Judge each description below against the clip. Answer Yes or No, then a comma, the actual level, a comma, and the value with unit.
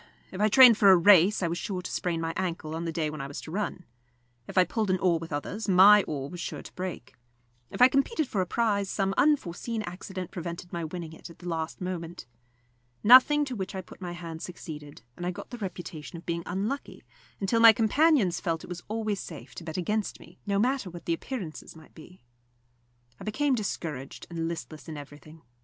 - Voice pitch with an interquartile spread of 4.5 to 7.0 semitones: No, average, 4.1 semitones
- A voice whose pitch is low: No, medium, 180 Hz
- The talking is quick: Yes, fast, 220 wpm